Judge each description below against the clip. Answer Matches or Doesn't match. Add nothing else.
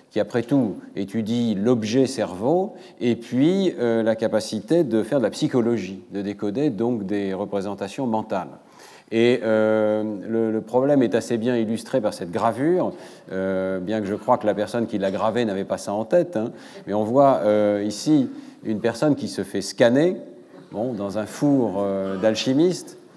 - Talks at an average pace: Matches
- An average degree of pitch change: Matches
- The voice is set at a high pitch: Doesn't match